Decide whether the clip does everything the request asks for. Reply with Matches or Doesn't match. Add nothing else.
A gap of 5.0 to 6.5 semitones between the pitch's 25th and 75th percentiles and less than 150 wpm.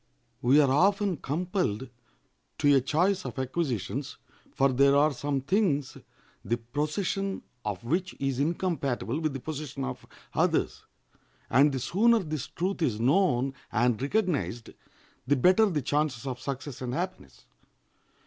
Matches